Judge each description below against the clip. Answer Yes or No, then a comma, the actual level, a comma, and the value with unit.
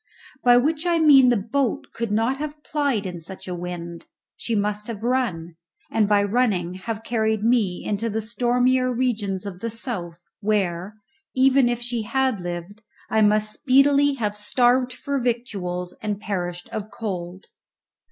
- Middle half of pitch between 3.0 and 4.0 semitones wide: No, average, 4.4 semitones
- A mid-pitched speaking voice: No, high, 220 Hz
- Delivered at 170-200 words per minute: No, average, 160 wpm